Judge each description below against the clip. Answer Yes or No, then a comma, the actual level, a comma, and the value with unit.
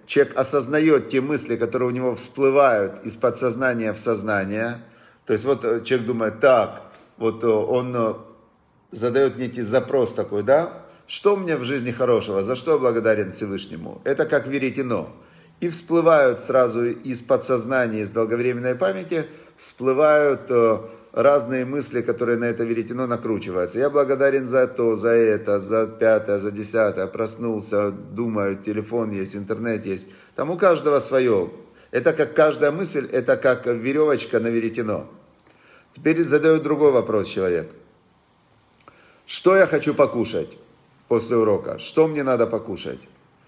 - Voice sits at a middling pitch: No, low, 120 Hz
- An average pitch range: Yes, average, 3.9 semitones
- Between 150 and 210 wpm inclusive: No, average, 135 wpm